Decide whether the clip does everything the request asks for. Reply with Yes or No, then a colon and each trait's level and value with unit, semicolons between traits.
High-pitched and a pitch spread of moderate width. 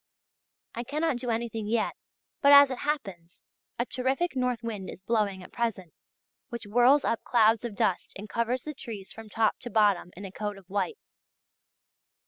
Yes: high, 230 Hz; average, 3.5 semitones